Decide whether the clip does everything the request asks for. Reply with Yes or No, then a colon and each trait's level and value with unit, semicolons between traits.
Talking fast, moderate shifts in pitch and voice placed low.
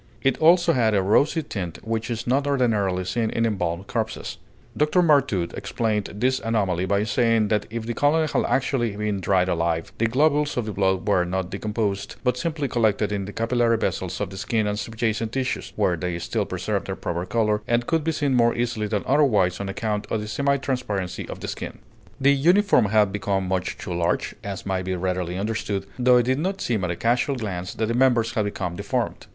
Yes: fast, 210 wpm; average, 4.5 semitones; low, 110 Hz